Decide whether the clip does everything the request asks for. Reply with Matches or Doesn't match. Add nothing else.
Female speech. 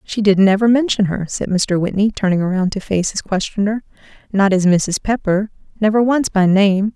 Matches